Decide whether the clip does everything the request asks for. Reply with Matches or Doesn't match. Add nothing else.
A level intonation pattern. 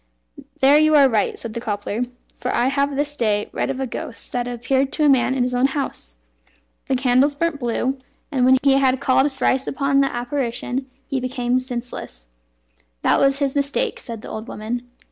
Matches